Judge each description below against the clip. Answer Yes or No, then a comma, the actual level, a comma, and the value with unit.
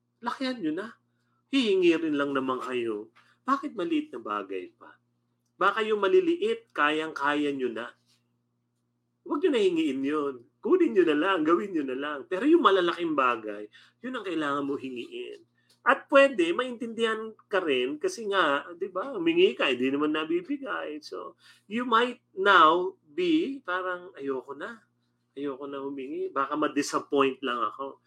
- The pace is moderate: Yes, average, 150 wpm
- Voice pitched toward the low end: No, medium, 180 Hz